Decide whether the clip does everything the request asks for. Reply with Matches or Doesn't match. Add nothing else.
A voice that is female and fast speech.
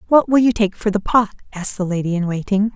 Matches